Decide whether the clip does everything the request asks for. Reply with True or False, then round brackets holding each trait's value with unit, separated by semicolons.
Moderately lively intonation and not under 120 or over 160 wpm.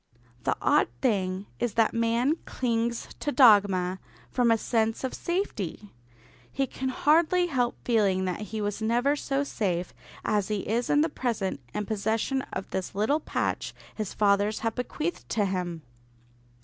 True (4.3 semitones; 155 wpm)